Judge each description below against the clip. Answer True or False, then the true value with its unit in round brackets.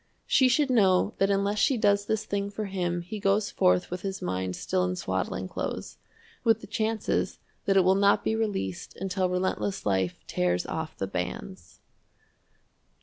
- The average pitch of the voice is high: True (195 Hz)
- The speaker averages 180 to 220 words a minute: False (170 wpm)